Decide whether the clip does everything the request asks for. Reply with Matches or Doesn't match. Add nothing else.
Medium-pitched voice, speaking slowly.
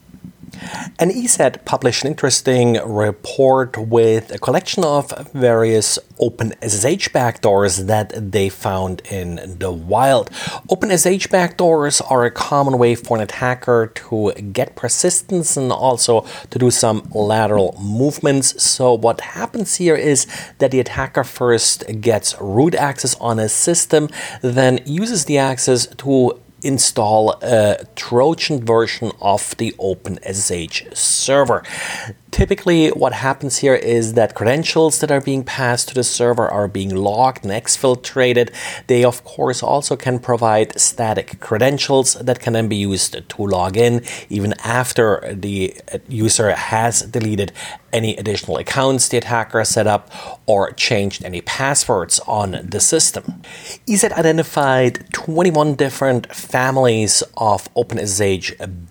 Doesn't match